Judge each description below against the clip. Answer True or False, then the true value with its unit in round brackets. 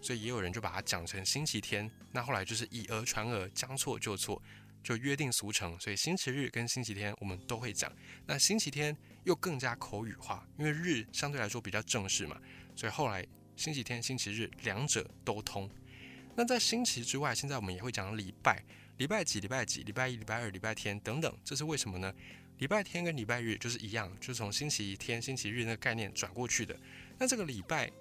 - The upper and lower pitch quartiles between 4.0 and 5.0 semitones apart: True (4.6 semitones)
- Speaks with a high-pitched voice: False (115 Hz)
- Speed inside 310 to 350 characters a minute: True (325 characters per minute)